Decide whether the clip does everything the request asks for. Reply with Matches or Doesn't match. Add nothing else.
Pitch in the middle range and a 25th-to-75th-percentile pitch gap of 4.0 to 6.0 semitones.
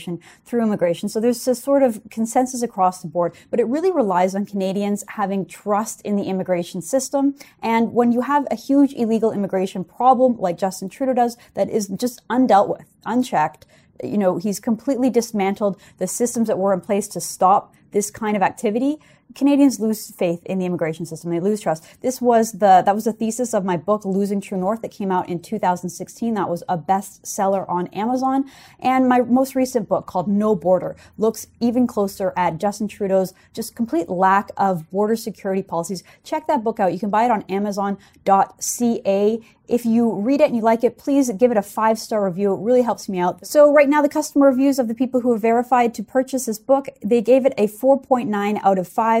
Doesn't match